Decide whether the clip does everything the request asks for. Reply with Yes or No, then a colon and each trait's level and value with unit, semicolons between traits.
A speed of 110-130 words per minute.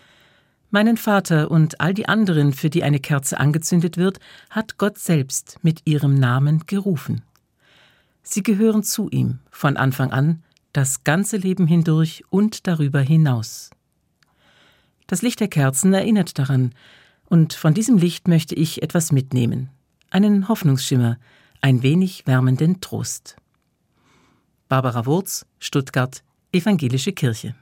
Yes: slow, 125 wpm